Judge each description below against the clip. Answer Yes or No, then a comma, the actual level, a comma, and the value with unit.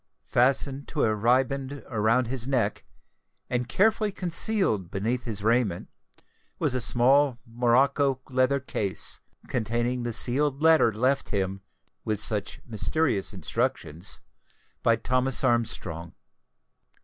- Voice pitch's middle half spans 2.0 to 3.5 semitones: No, average, 3.9 semitones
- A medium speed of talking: No, slow, 115 wpm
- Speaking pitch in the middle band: No, low, 125 Hz